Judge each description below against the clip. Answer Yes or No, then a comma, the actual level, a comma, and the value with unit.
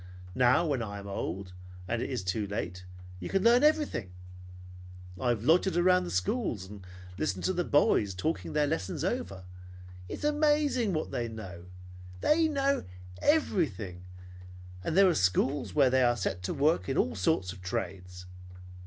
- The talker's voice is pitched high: No, low, 120 Hz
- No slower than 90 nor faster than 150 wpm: No, average, 170 wpm